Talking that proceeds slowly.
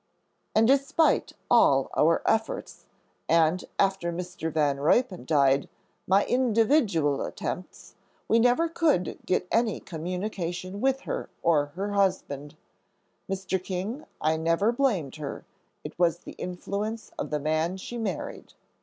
Yes: slow, 130 wpm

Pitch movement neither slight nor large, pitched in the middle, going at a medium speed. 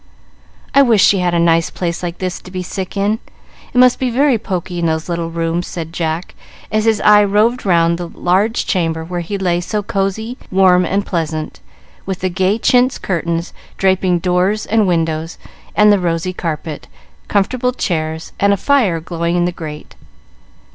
Yes: average, 3.5 semitones; medium, 180 Hz; average, 175 wpm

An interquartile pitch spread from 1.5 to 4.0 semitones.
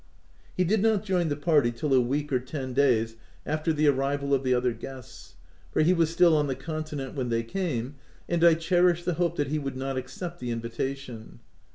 No: average, 4.4 semitones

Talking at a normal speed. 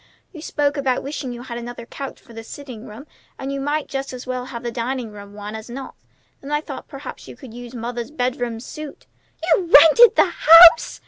No: fast, 210 wpm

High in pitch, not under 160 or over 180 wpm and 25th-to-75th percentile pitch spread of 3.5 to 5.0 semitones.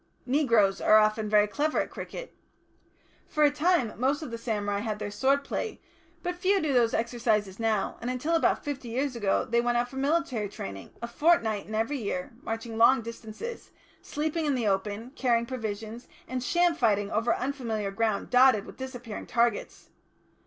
Yes: high, 235 Hz; average, 175 wpm; average, 4.4 semitones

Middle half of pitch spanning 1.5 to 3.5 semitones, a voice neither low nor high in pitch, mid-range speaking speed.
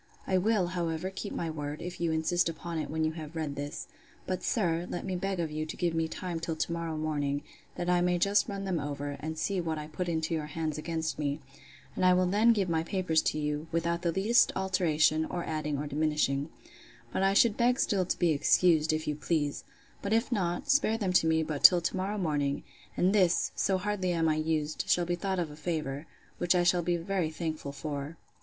No: average, 2.9 semitones; medium, 165 Hz; fast, 225 wpm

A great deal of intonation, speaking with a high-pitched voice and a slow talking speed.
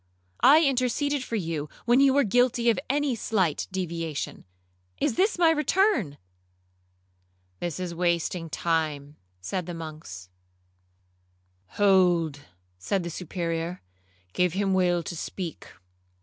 No: wide, 6.7 semitones; medium, 180 Hz; slow, 115 wpm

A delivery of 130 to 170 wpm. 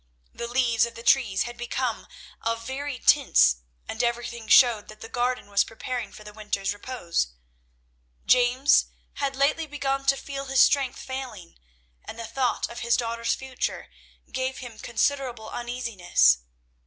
Yes: average, 150 wpm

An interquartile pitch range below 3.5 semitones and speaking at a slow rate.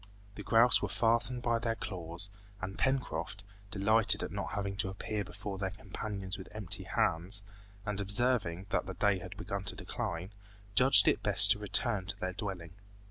No: narrow, 2.5 semitones; average, 175 wpm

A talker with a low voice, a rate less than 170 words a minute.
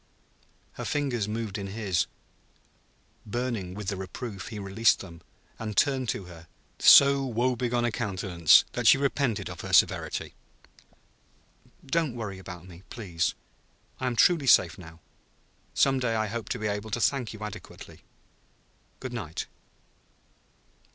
Yes: low, 110 Hz; average, 140 wpm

